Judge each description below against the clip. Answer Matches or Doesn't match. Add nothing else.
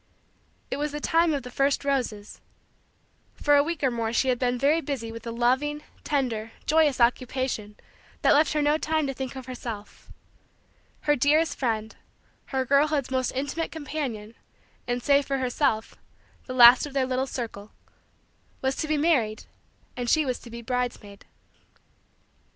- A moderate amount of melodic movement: Matches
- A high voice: Matches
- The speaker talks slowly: Doesn't match